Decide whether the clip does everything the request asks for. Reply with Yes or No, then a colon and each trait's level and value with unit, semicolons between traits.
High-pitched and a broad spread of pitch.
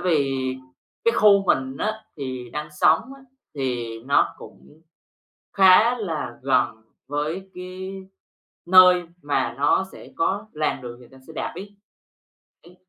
No: medium, 160 Hz; wide, 6.1 semitones